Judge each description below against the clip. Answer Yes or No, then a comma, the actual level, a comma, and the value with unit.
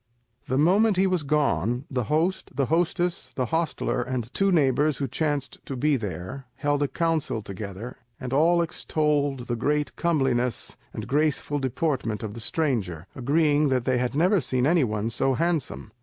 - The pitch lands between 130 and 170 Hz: Yes, medium, 140 Hz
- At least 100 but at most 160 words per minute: No, average, 170 wpm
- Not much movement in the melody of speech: No, average, 4.3 semitones